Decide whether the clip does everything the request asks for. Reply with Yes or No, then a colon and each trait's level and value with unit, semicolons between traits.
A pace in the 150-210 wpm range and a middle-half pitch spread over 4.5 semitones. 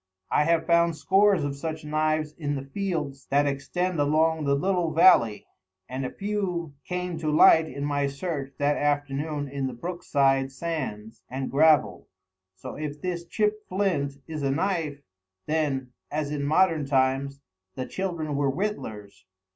No: average, 155 wpm; average, 3.4 semitones